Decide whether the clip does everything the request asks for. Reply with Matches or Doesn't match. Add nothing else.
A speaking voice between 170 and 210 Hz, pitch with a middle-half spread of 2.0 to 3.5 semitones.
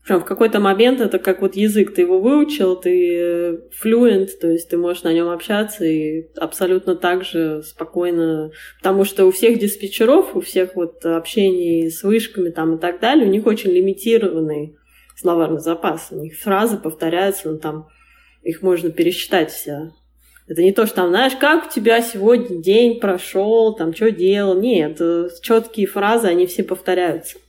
Doesn't match